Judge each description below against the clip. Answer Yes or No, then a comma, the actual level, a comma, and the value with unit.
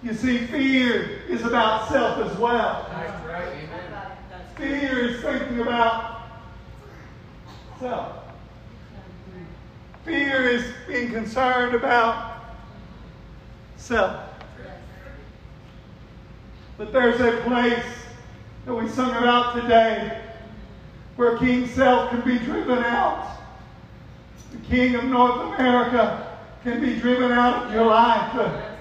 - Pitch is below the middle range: No, high, 240 Hz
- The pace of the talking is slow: Yes, slow, 100 wpm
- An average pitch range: No, narrow, 1.5 semitones